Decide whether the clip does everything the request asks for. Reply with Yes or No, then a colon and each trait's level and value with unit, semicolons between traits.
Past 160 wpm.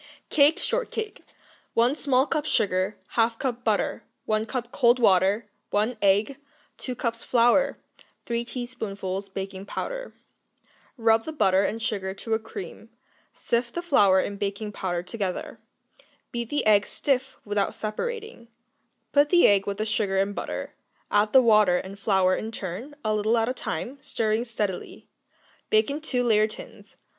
No: average, 155 wpm